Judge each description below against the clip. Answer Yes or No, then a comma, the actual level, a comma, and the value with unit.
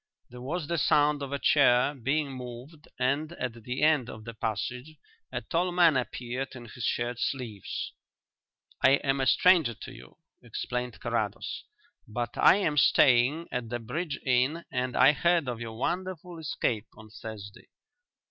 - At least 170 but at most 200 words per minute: No, average, 160 wpm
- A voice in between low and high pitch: No, low, 130 Hz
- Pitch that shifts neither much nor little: Yes, average, 4.1 semitones